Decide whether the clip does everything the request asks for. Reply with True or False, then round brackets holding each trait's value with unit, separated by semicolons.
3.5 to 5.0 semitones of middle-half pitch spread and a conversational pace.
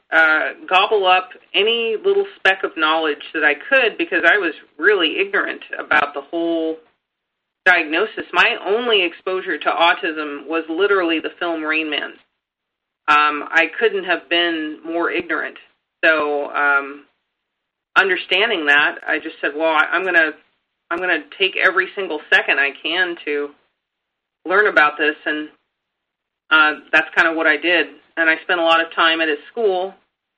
True (3.9 semitones; 160 wpm)